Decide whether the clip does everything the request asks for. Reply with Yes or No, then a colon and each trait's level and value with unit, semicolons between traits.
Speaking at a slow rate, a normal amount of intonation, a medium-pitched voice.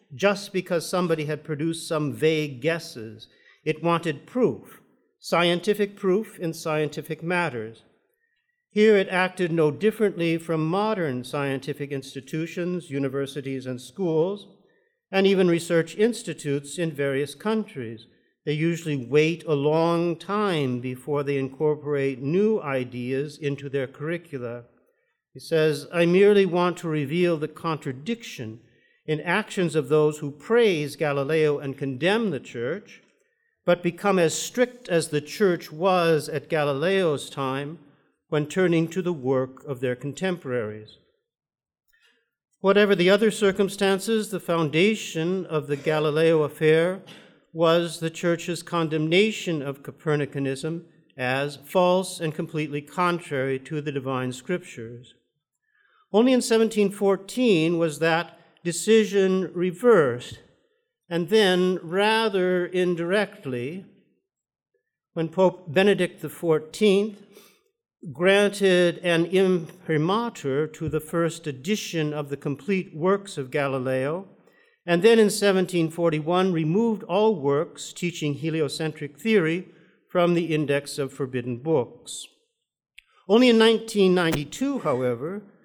Yes: slow, 115 wpm; average, 4.8 semitones; medium, 165 Hz